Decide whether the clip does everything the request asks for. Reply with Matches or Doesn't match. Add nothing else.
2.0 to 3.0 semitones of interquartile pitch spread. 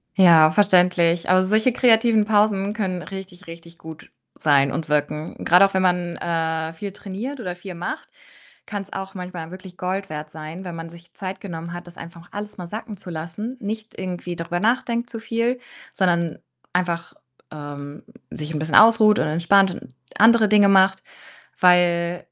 Doesn't match